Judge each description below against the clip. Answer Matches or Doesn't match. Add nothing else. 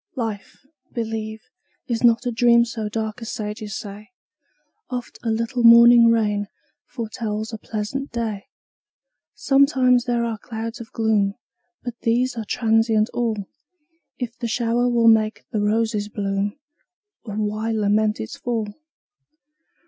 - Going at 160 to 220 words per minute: Doesn't match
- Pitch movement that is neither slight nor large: Doesn't match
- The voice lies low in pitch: Doesn't match